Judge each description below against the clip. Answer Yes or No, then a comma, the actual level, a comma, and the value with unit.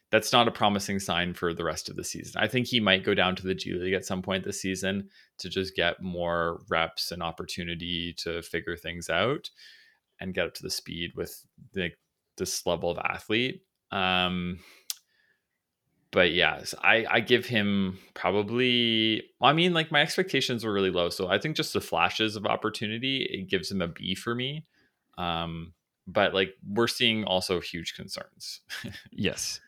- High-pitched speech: No, very low, 95 Hz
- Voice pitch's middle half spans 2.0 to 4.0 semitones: No, average, 4.9 semitones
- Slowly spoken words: No, average, 185 wpm